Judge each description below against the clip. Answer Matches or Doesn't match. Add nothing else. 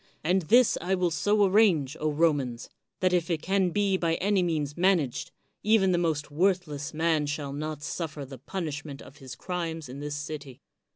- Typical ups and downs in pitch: Matches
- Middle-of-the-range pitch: Matches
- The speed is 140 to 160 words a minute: Doesn't match